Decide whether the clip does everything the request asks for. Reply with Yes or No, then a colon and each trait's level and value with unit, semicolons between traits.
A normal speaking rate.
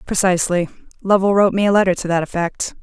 Yes: average, 190 wpm